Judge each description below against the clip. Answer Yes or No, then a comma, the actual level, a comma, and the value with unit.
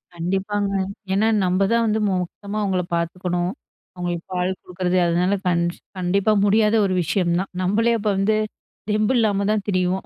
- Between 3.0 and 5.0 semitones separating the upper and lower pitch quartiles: No, narrow, 2.6 semitones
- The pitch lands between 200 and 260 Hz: No, high, 190 Hz